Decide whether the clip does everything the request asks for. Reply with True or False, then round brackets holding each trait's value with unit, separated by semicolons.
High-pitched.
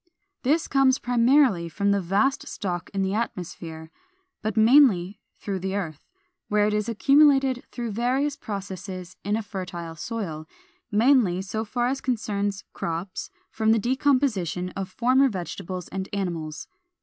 True (205 Hz)